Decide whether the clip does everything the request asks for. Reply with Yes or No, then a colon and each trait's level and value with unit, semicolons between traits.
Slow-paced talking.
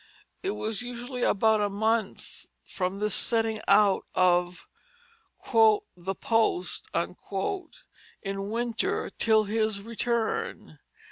Yes: slow, 95 wpm